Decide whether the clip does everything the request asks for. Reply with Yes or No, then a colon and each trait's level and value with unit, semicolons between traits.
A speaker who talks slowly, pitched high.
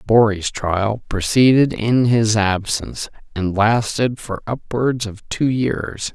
No: slow, 125 wpm; low, 110 Hz